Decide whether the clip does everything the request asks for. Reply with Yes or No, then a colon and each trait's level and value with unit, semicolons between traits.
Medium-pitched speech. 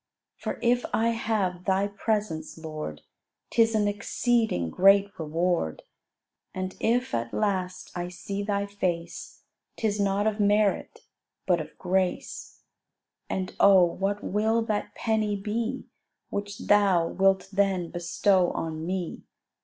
No: high, 200 Hz